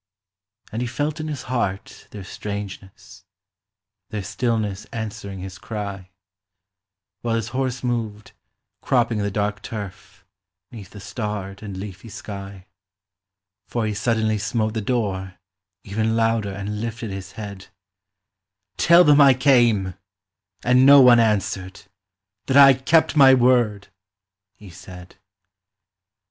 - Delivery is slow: Yes, slow, 125 wpm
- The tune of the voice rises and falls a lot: No, average, 3.4 semitones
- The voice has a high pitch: No, low, 110 Hz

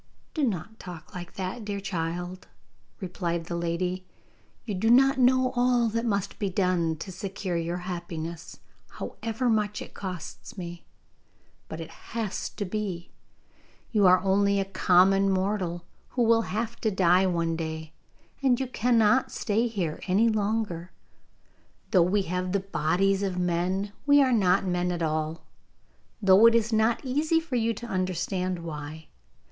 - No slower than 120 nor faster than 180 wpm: Yes, average, 155 wpm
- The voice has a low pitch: No, high, 190 Hz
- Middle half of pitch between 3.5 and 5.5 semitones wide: Yes, average, 4.0 semitones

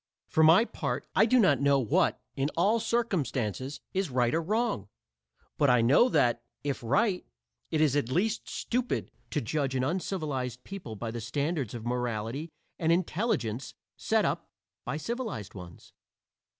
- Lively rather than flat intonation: Yes, wide, 7.4 semitones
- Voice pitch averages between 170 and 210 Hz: No, medium, 145 Hz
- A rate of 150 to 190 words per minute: Yes, average, 155 wpm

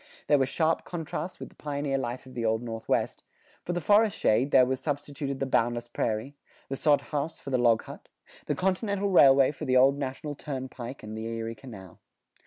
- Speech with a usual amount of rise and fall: Yes, average, 3.8 semitones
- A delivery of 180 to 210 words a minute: Yes, average, 195 wpm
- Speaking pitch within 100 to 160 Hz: Yes, low, 135 Hz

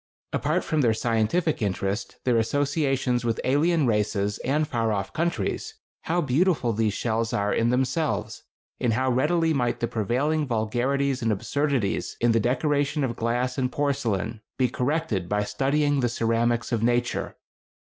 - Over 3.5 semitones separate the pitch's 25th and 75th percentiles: Yes, average, 4.0 semitones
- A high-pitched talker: No, low, 125 Hz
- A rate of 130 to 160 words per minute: Yes, average, 150 wpm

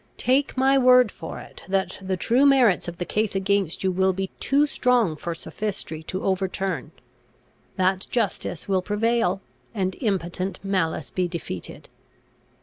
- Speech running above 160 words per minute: No, average, 145 wpm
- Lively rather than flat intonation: No, average, 3.9 semitones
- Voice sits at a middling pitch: No, high, 195 Hz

